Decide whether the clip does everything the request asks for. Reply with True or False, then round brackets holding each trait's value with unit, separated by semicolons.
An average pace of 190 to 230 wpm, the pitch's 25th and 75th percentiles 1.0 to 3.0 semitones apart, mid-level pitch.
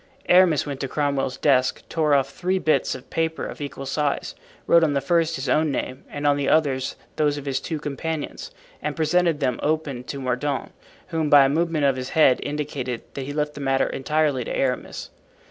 True (200 wpm; 2.6 semitones; 145 Hz)